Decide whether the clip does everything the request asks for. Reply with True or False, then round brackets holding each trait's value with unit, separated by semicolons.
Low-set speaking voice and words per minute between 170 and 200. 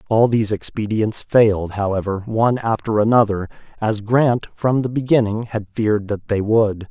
False (110 Hz; 155 wpm)